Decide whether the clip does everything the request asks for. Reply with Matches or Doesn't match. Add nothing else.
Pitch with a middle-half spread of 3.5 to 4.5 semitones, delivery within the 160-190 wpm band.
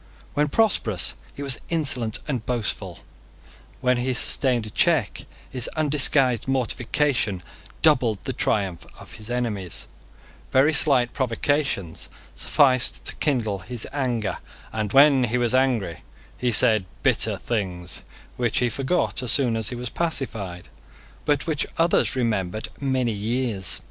Doesn't match